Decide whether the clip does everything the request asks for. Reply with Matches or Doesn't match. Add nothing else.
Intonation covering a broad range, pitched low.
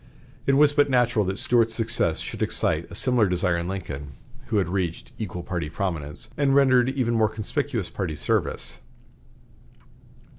Matches